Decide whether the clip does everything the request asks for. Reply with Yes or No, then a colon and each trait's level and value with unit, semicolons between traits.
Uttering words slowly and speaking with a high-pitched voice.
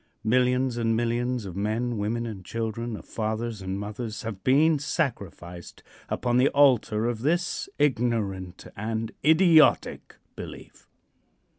No: slow, 125 wpm; low, 115 Hz